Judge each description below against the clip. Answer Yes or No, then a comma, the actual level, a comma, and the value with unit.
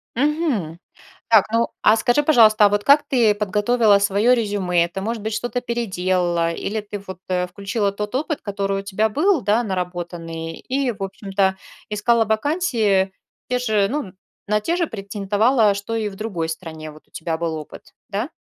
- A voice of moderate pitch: No, high, 205 Hz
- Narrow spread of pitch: No, average, 3.7 semitones